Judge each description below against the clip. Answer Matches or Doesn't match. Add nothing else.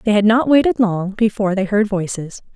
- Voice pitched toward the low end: Doesn't match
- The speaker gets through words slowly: Doesn't match